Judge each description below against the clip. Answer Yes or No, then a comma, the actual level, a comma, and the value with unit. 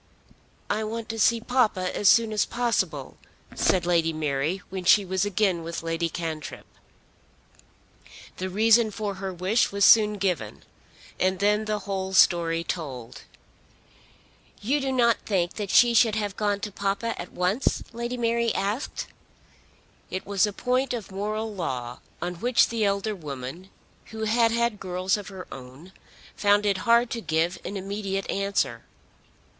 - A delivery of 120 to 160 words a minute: Yes, average, 155 wpm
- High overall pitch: Yes, high, 200 Hz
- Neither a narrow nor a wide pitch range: Yes, average, 3.6 semitones